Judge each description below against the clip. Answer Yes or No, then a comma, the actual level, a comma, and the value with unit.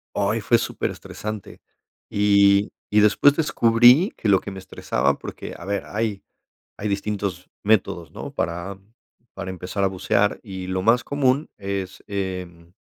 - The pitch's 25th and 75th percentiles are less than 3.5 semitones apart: Yes, narrow, 2.4 semitones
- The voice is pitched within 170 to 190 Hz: No, low, 100 Hz